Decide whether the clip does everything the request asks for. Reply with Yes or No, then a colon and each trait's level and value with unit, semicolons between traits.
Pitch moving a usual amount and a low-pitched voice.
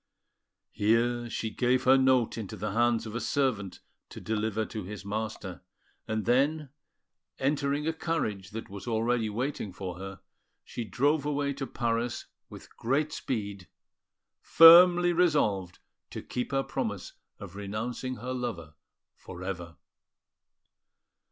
Yes: average, 4.7 semitones; low, 115 Hz